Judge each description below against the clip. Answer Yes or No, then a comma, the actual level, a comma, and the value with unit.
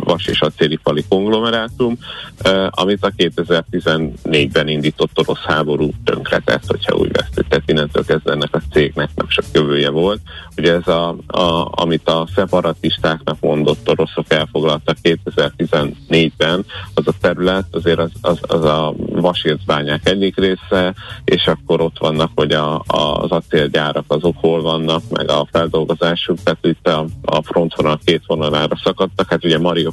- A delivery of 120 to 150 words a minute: Yes, average, 145 wpm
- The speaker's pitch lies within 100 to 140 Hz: No, very low, 80 Hz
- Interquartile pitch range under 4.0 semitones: Yes, average, 2.8 semitones